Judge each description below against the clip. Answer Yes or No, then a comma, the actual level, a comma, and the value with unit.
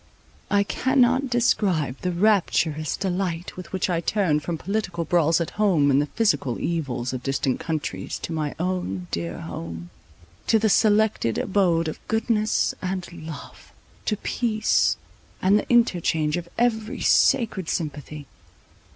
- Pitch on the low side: No, medium, 175 Hz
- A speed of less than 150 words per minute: Yes, average, 140 wpm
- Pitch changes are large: Yes, wide, 5.8 semitones